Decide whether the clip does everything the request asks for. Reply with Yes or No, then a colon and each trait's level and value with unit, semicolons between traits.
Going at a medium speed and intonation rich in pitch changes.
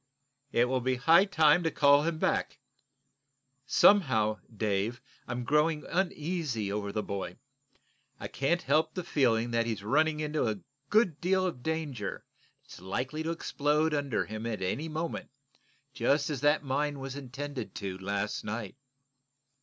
Yes: average, 150 wpm; wide, 5.8 semitones